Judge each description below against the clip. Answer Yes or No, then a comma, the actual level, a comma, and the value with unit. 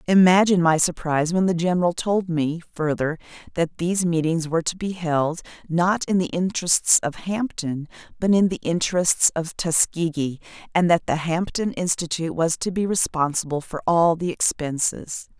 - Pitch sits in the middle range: Yes, medium, 170 Hz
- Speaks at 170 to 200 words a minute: No, average, 160 wpm